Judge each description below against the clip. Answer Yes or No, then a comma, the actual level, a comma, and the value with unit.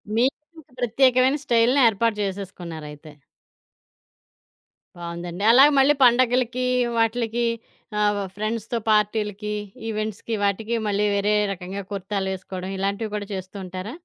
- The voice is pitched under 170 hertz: No, high, 210 Hz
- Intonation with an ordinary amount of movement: Yes, average, 3.5 semitones